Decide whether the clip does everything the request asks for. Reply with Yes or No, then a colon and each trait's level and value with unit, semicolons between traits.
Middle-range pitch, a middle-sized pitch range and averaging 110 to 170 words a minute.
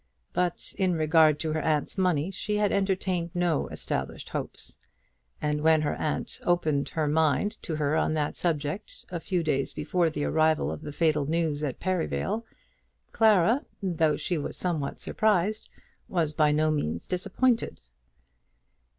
Yes: medium, 160 Hz; average, 3.3 semitones; average, 150 wpm